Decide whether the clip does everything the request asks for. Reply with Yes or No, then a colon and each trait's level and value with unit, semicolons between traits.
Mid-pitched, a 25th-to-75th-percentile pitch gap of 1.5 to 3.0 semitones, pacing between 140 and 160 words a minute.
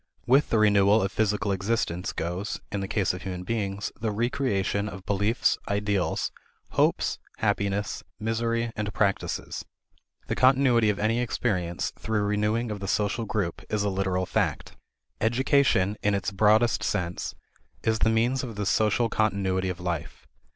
No: low, 105 Hz; narrow, 2.5 semitones; average, 150 wpm